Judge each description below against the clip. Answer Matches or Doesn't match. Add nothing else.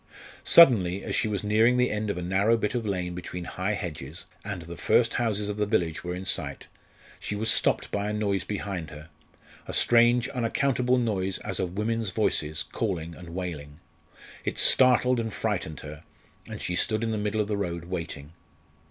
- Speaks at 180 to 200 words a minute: Matches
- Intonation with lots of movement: Doesn't match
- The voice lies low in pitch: Matches